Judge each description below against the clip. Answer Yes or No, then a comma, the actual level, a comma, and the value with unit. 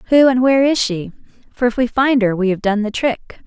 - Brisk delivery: Yes, fast, 260 wpm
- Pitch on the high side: Yes, high, 235 Hz